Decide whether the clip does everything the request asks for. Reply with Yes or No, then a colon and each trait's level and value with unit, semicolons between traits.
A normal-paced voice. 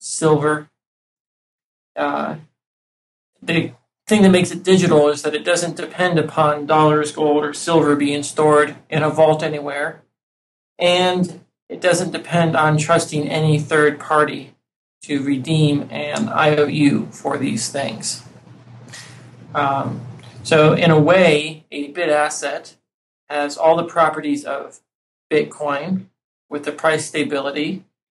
No: slow, 125 wpm